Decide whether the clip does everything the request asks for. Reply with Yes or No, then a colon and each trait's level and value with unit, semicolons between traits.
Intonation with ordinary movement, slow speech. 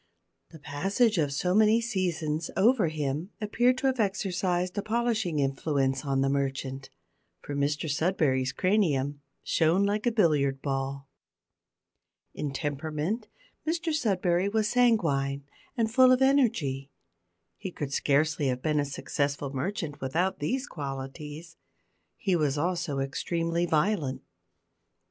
No: wide, 6.5 semitones; slow, 125 wpm